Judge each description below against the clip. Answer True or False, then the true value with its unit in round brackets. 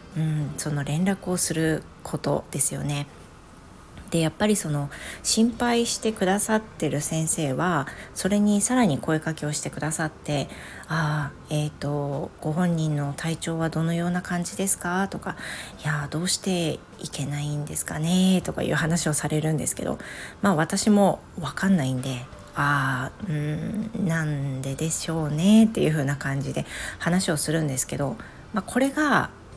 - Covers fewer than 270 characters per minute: False (315 characters per minute)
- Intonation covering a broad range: False (4.3 semitones)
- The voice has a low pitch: False (160 Hz)